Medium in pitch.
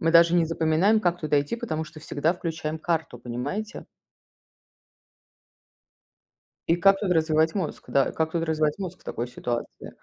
Yes: medium, 160 Hz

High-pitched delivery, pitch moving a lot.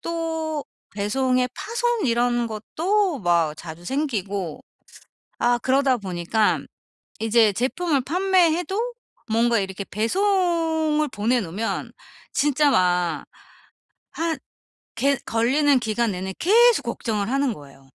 Yes: very high, 250 Hz; wide, 7.6 semitones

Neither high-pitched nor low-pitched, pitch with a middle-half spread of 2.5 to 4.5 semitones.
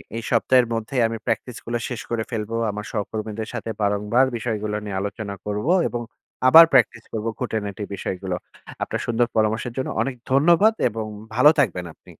No: low, 110 Hz; average, 2.8 semitones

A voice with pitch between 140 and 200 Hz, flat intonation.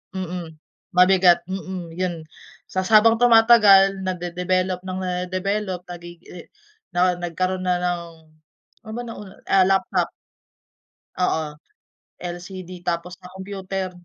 Yes: medium, 185 Hz; narrow, 1.4 semitones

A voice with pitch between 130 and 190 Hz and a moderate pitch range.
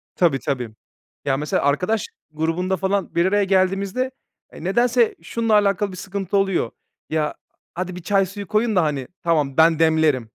Yes: medium, 185 Hz; average, 4.1 semitones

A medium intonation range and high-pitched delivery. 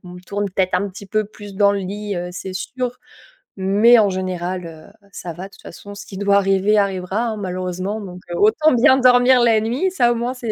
Yes: average, 3.6 semitones; high, 200 Hz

